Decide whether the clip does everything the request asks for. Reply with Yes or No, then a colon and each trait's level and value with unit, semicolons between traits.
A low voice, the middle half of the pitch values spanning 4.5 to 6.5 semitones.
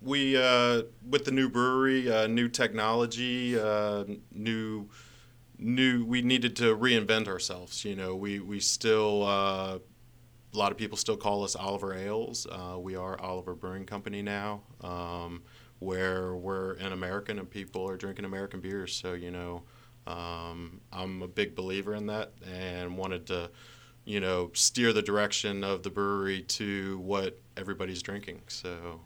No: low, 100 Hz; average, 3.7 semitones